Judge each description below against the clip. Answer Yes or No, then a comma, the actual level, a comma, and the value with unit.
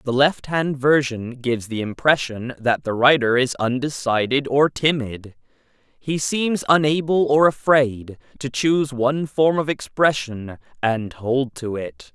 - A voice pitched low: Yes, low, 130 Hz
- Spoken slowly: No, average, 145 wpm